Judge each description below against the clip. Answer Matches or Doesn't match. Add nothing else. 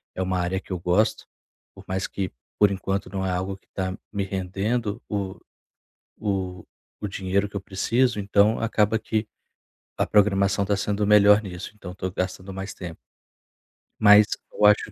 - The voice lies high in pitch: Doesn't match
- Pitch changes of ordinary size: Doesn't match